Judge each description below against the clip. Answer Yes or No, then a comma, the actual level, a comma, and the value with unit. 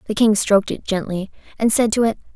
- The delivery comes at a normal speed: No, fast, 230 wpm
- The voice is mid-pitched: No, high, 210 Hz